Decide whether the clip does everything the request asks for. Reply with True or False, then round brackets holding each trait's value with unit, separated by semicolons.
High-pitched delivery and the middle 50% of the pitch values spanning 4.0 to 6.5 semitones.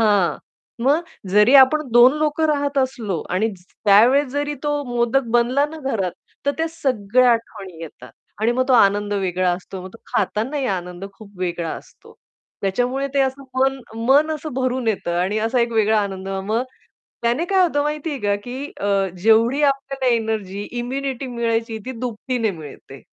True (235 Hz; 5.2 semitones)